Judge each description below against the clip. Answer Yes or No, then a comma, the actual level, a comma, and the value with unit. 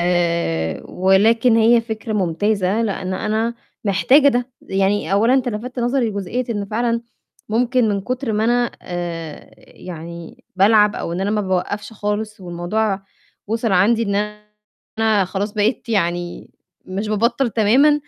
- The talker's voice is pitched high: Yes, high, 210 Hz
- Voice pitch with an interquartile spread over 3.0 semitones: Yes, average, 3.5 semitones